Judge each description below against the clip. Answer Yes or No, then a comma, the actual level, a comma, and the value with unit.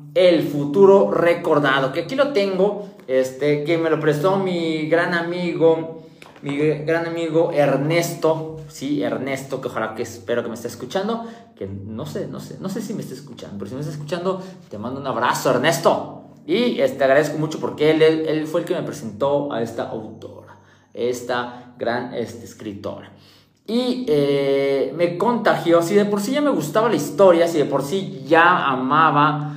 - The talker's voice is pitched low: No, medium, 155 Hz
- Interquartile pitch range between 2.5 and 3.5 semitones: No, average, 4.2 semitones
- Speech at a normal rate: Yes, average, 180 wpm